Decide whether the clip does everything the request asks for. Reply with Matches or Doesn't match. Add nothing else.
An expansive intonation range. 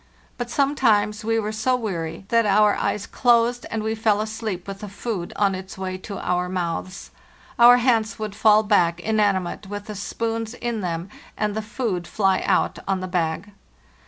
Doesn't match